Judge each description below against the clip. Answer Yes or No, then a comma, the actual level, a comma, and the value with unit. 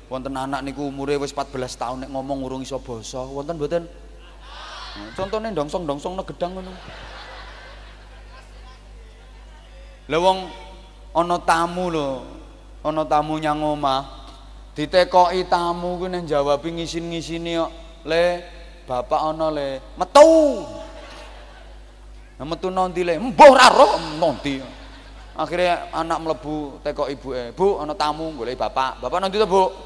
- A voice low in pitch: No, medium, 155 Hz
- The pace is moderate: Yes, average, 125 wpm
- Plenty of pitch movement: No, average, 4.7 semitones